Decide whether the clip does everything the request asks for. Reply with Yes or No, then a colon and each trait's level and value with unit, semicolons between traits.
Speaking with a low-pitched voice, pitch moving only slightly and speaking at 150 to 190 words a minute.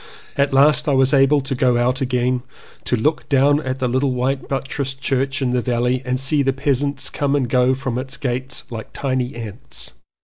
No: low, 130 Hz; narrow, 1.7 semitones; average, 200 wpm